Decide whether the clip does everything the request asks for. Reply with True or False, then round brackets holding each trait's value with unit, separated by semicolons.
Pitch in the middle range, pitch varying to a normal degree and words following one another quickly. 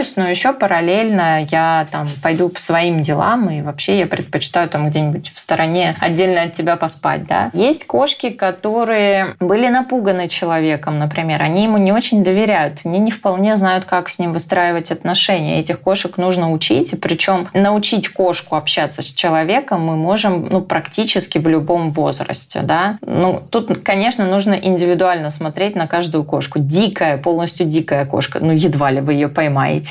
True (175 Hz; 3.4 semitones; 165 wpm)